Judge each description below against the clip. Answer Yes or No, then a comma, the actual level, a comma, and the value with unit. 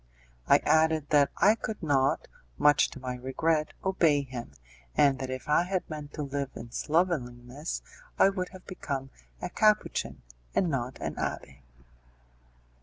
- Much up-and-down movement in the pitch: No, average, 4.4 semitones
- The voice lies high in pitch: No, medium, 145 Hz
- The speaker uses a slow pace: No, average, 150 wpm